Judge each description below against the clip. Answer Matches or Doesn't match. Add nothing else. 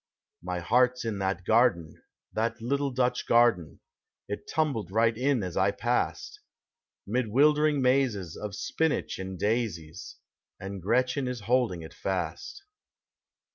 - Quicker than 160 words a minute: Doesn't match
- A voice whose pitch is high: Doesn't match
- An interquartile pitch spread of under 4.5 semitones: Doesn't match